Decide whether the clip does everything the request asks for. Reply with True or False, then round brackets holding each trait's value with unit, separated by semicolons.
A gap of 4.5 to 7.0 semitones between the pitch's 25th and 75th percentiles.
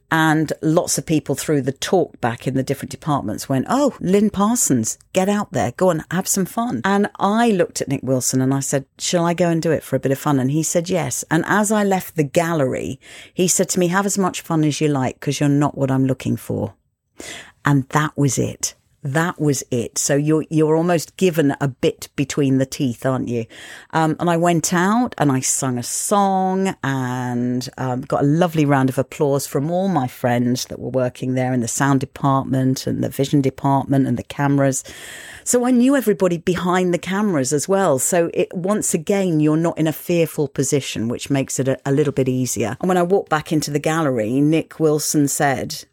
True (4.8 semitones)